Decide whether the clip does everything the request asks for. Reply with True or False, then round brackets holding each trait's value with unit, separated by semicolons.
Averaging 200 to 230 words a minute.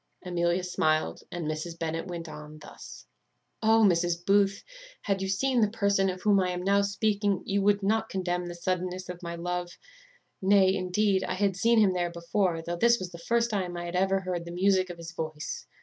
True (205 wpm)